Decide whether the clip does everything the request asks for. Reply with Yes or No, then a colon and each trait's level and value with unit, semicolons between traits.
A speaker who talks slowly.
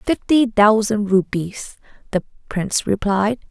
Yes: slow, 105 wpm